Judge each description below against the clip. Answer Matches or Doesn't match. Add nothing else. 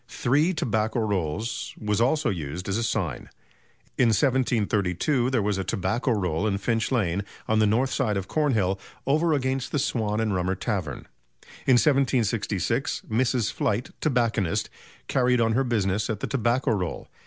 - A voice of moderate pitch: Doesn't match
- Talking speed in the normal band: Matches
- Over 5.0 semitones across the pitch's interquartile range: Doesn't match